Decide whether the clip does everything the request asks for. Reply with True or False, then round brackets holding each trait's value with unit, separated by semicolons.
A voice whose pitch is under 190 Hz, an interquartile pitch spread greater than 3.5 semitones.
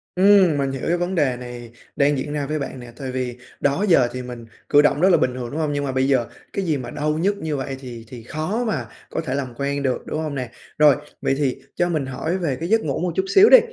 True (140 Hz; 4.2 semitones)